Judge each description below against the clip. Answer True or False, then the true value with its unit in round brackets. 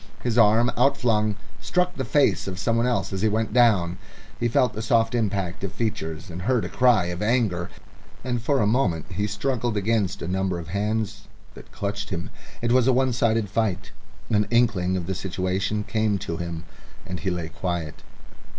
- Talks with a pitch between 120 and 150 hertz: False (105 Hz)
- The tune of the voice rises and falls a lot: False (4.1 semitones)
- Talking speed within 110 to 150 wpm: False (185 wpm)